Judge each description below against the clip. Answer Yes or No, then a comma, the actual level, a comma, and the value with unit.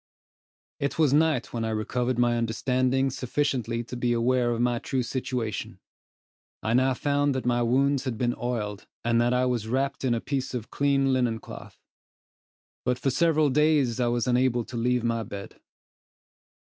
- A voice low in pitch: Yes, low, 125 Hz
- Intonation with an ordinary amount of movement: No, narrow, 2.2 semitones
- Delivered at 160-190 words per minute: Yes, average, 170 wpm